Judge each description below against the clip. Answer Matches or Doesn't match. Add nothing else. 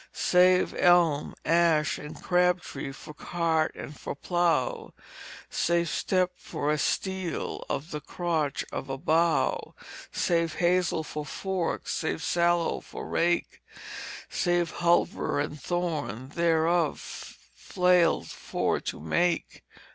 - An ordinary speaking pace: Doesn't match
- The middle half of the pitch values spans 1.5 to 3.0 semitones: Matches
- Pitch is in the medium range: Matches